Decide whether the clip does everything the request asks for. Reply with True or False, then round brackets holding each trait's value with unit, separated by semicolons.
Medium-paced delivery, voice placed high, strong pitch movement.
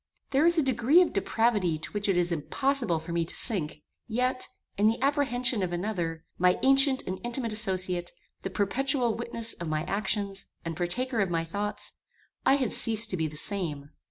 True (185 wpm; 205 Hz; 6.0 semitones)